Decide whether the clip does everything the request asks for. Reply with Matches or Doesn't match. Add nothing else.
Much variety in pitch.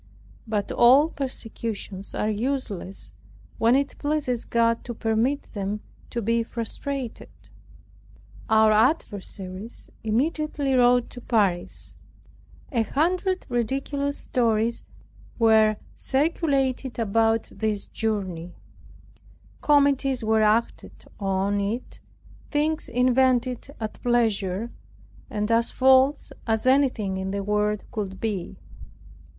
Doesn't match